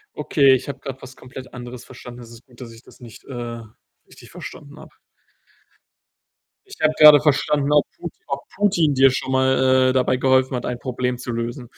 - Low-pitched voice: Yes, low, 130 Hz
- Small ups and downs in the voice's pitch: Yes, narrow, 2.2 semitones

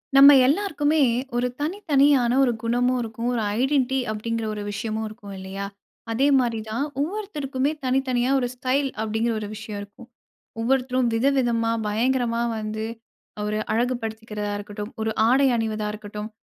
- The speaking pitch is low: No, high, 235 Hz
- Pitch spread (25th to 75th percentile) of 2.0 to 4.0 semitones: Yes, average, 3.5 semitones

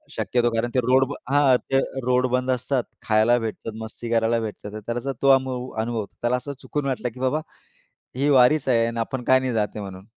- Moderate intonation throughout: No, narrow, 2.3 semitones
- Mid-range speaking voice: No, low, 125 Hz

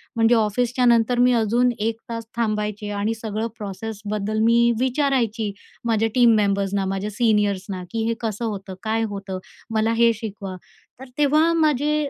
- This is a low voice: No, high, 225 Hz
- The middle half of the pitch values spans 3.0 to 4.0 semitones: No, narrow, 2.5 semitones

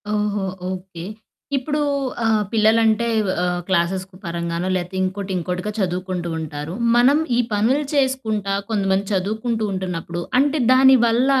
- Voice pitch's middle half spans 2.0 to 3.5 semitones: No, average, 4.1 semitones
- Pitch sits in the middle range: No, high, 200 Hz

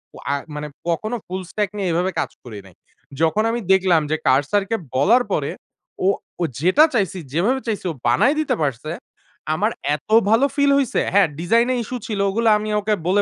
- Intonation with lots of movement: Yes, wide, 5.8 semitones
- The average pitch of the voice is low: No, high, 195 Hz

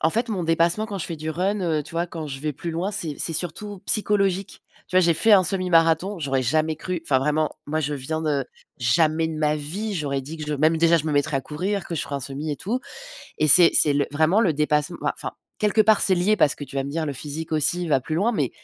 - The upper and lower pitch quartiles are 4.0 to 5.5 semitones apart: No, average, 3.6 semitones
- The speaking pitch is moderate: Yes, medium, 160 Hz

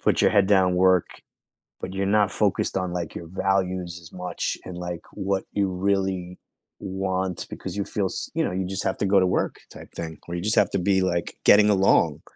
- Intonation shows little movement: Yes, narrow, 1.5 semitones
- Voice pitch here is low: Yes, very low, 95 Hz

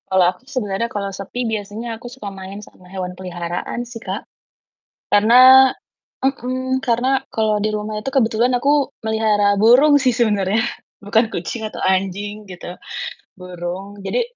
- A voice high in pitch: Yes, high, 215 Hz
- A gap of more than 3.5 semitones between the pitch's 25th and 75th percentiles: Yes, average, 4.0 semitones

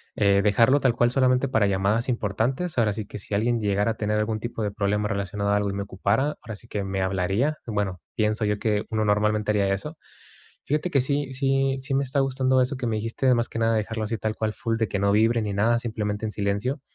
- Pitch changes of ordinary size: Yes, average, 3.6 semitones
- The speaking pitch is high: No, low, 110 Hz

